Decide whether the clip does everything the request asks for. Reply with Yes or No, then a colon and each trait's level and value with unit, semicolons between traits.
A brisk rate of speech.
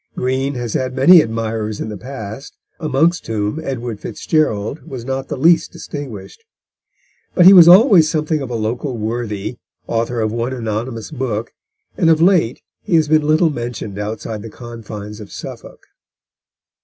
No: average, 155 wpm